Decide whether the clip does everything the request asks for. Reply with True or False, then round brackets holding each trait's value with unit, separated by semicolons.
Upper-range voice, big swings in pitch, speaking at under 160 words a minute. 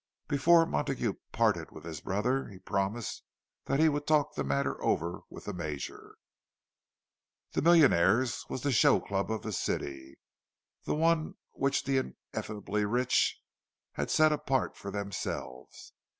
False (115 Hz; 7.0 semitones; 140 wpm)